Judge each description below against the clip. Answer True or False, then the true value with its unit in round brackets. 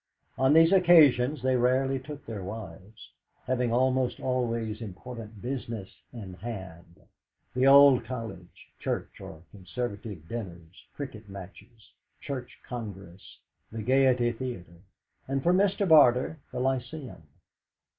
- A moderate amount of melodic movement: True (4.4 semitones)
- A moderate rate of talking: False (115 wpm)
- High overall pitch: False (120 Hz)